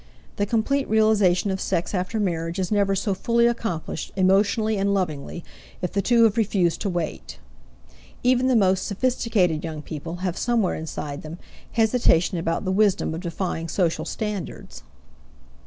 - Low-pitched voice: No, high, 190 Hz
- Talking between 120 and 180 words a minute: Yes, average, 155 wpm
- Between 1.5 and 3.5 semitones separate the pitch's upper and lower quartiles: No, average, 4.4 semitones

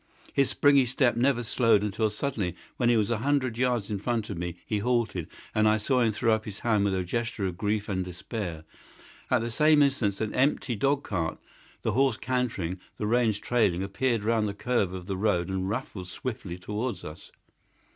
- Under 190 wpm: No, average, 200 wpm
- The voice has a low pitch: Yes, low, 110 Hz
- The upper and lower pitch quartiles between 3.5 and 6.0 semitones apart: Yes, average, 4.0 semitones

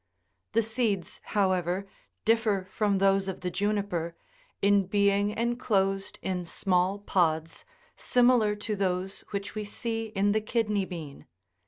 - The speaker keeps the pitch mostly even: Yes, narrow, 2.2 semitones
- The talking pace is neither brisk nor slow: No, slow, 130 wpm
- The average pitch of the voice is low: No, high, 200 Hz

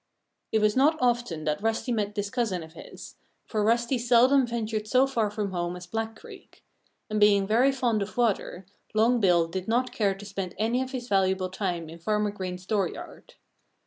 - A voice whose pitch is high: Yes, high, 210 Hz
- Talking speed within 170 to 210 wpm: Yes, average, 190 wpm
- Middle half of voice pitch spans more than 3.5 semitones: Yes, average, 3.9 semitones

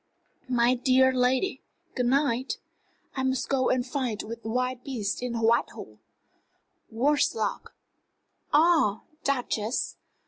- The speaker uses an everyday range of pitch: No, narrow, 2.1 semitones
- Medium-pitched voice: No, very high, 250 Hz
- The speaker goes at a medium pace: No, slow, 110 wpm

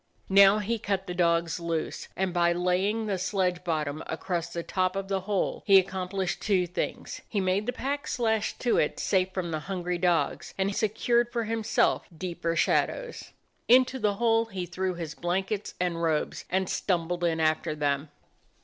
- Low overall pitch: No, medium, 185 Hz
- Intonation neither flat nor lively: Yes, average, 3.1 semitones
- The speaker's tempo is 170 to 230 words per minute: Yes, average, 175 wpm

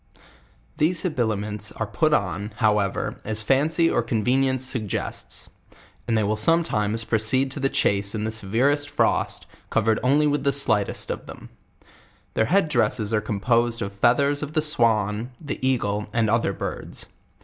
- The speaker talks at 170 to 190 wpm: No, average, 155 wpm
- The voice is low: Yes, low, 115 Hz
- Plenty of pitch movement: No, average, 4.5 semitones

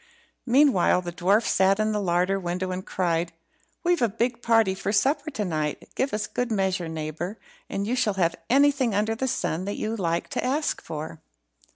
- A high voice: Yes, high, 200 Hz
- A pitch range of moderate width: Yes, average, 5.0 semitones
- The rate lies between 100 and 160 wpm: No, average, 190 wpm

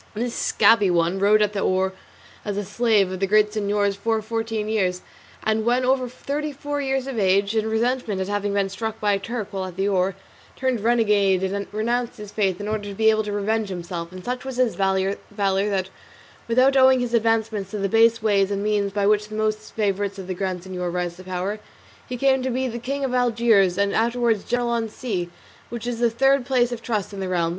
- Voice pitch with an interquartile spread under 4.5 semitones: Yes, average, 3.3 semitones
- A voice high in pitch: Yes, high, 210 Hz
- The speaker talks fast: Yes, fast, 220 wpm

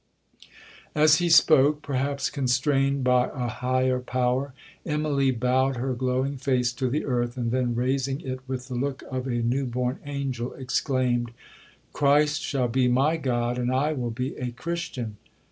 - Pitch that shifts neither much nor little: No, narrow, 2.0 semitones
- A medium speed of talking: Yes, average, 160 wpm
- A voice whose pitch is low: Yes, low, 130 Hz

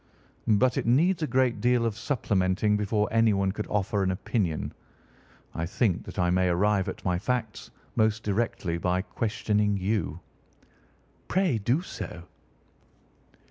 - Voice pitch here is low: Yes, low, 105 Hz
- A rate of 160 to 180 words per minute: No, average, 140 wpm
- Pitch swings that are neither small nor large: Yes, average, 3.8 semitones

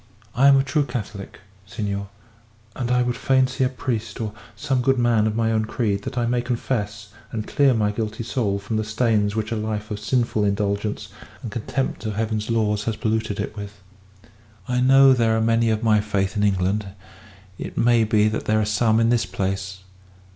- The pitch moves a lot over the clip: No, narrow, 2.4 semitones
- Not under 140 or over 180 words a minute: No, average, 200 wpm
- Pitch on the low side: Yes, low, 110 Hz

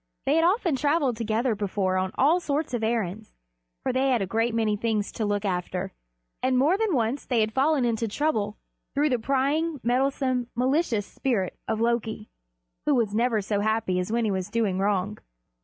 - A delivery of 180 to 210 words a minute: Yes, average, 190 wpm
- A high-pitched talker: Yes, high, 230 Hz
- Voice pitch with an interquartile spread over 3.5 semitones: Yes, average, 4.5 semitones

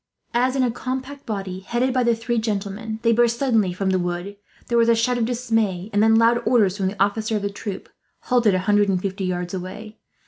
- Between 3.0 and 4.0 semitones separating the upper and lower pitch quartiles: Yes, average, 3.4 semitones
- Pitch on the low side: No, high, 220 Hz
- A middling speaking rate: No, fast, 230 wpm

